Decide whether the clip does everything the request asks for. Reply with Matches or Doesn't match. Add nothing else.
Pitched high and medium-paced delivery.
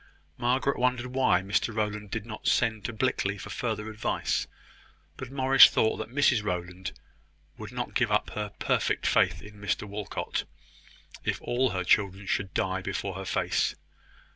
Doesn't match